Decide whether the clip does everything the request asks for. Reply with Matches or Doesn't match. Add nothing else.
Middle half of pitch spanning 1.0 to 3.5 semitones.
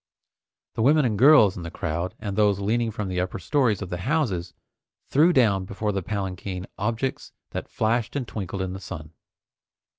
Doesn't match